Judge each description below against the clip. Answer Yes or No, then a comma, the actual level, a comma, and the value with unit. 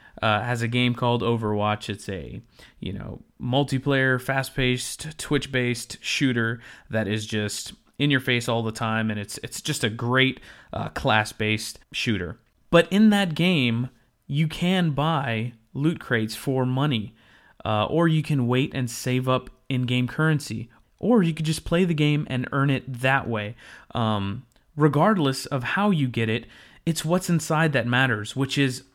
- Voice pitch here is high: No, low, 130 Hz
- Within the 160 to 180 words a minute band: Yes, average, 165 wpm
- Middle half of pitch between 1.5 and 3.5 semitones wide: No, average, 4.3 semitones